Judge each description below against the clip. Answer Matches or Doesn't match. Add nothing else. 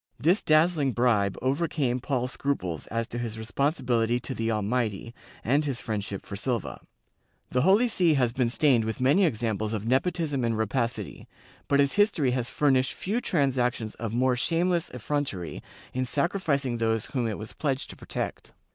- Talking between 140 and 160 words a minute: Doesn't match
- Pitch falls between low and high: Doesn't match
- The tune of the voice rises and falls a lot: Doesn't match